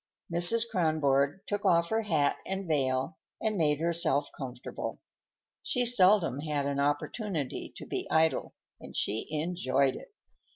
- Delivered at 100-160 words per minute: Yes, slow, 135 wpm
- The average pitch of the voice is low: No, medium, 160 Hz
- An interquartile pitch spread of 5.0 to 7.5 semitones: Yes, average, 5.3 semitones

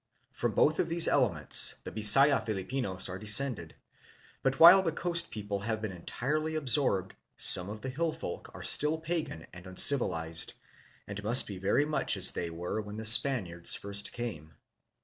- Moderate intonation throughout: No, wide, 7.1 semitones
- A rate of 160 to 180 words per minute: Yes, average, 170 wpm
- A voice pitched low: Yes, low, 110 Hz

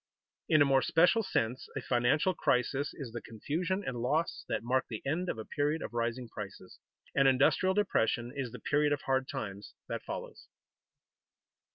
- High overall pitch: No, low, 135 Hz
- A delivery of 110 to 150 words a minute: No, average, 175 wpm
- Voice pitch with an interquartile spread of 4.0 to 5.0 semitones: Yes, average, 4.6 semitones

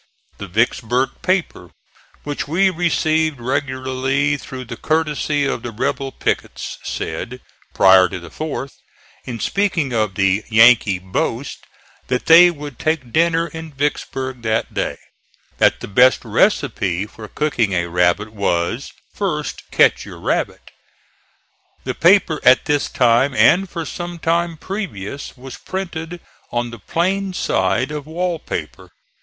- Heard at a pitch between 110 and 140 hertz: Yes, low, 135 Hz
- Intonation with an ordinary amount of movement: No, wide, 6.2 semitones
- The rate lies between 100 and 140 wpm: Yes, slow, 135 wpm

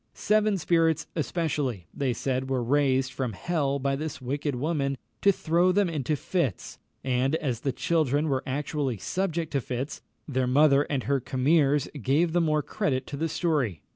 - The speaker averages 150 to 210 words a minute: Yes, average, 170 wpm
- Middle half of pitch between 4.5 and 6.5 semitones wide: No, average, 3.6 semitones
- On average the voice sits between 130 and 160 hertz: Yes, medium, 140 Hz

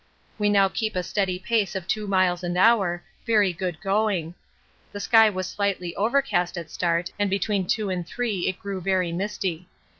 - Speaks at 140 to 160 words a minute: No, average, 180 wpm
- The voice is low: No, high, 190 Hz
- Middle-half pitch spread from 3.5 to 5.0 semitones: No, average, 2.8 semitones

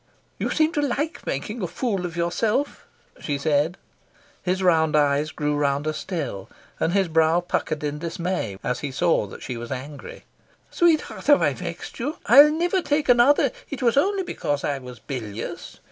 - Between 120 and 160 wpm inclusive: No, average, 175 wpm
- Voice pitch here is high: No, medium, 170 Hz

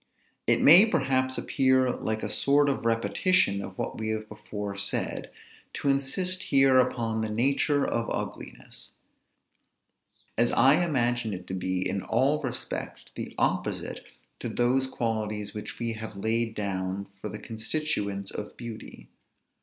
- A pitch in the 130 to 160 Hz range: No, low, 115 Hz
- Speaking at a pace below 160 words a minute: Yes, average, 145 wpm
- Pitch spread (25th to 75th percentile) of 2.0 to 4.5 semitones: Yes, average, 4.1 semitones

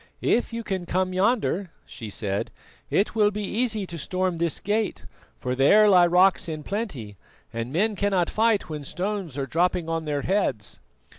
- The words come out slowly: No, average, 170 wpm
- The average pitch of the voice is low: No, medium, 185 Hz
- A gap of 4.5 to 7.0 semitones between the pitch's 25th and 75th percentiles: Yes, average, 5.3 semitones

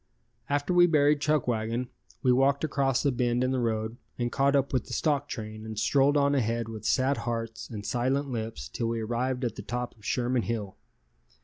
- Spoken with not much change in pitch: No, average, 3.4 semitones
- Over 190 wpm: Yes, average, 200 wpm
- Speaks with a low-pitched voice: Yes, low, 125 Hz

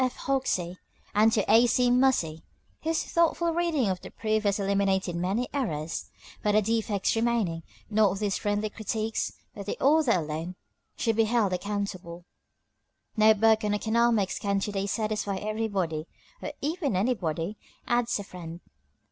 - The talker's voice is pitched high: Yes, high, 210 Hz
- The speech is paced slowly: No, average, 150 wpm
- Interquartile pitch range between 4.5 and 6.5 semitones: No, average, 3.6 semitones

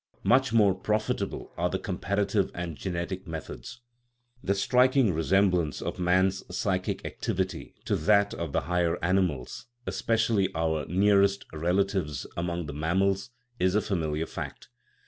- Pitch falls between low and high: No, very low, 95 Hz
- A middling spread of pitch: Yes, average, 3.0 semitones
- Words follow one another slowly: Yes, slow, 130 wpm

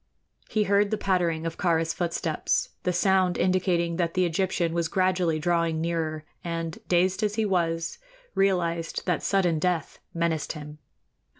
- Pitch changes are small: Yes, narrow, 2.1 semitones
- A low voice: No, medium, 170 Hz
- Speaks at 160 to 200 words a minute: No, average, 145 wpm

